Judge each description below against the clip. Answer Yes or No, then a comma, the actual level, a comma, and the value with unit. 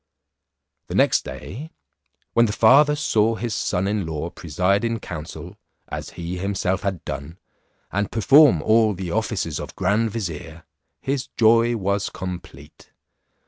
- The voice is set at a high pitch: No, low, 100 Hz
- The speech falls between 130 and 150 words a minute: Yes, average, 140 wpm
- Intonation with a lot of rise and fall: No, average, 4.7 semitones